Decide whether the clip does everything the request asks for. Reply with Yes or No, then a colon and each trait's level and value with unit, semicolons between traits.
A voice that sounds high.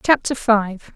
Yes: high, 230 Hz